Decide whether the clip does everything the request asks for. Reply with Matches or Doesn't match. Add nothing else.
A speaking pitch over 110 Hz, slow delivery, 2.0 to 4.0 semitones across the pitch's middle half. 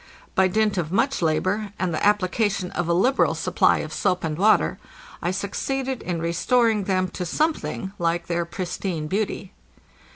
Doesn't match